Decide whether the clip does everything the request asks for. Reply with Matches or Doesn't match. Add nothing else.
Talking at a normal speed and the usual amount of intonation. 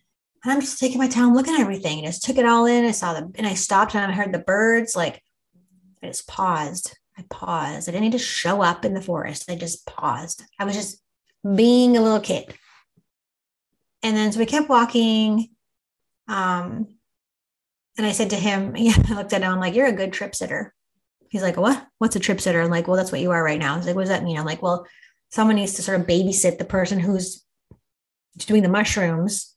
Doesn't match